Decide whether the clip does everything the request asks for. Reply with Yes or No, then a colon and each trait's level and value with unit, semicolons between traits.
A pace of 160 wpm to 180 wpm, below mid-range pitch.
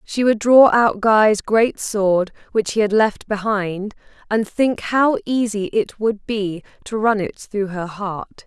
No: average, 175 wpm; high, 210 Hz